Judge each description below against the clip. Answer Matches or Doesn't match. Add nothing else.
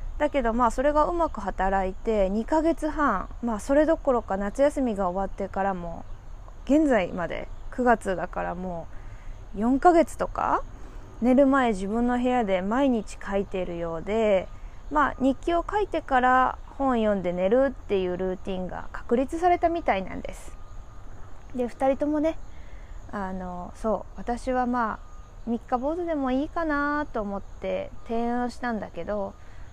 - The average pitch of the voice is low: Doesn't match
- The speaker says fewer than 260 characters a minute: Doesn't match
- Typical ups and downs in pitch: Doesn't match